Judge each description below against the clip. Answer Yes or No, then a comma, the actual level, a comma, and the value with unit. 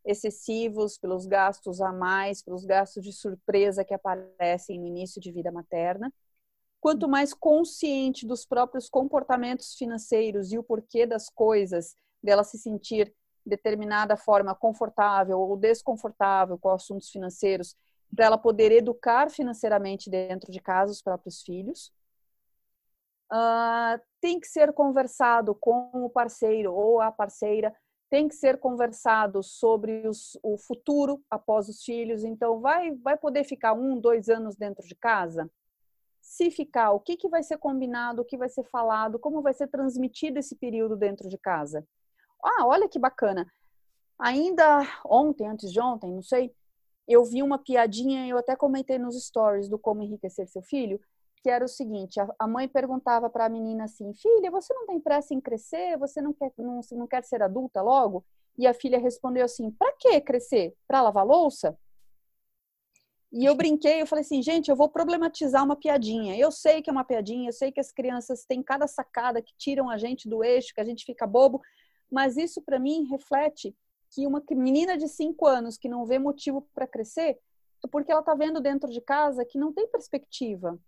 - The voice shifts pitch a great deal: No, average, 4.8 semitones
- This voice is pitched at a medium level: No, high, 240 Hz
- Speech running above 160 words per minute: Yes, average, 175 wpm